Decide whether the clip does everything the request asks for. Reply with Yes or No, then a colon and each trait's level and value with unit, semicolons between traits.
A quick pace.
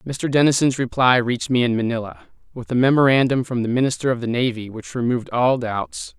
No: average, 195 wpm